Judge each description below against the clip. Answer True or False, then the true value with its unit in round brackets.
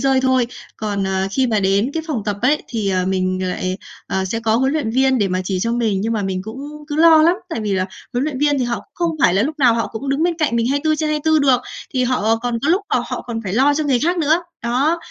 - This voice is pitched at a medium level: False (245 Hz)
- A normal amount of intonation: False (6.1 semitones)